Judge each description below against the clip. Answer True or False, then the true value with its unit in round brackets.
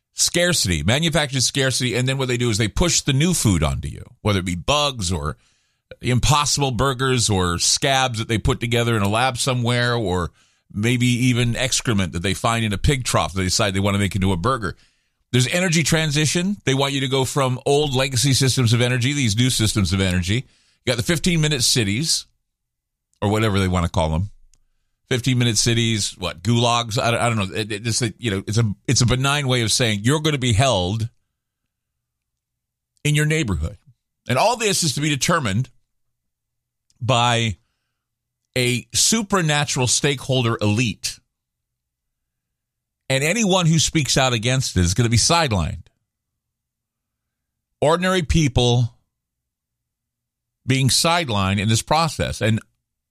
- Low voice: True (120 Hz)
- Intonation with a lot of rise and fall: False (4.2 semitones)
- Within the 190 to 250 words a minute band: False (170 wpm)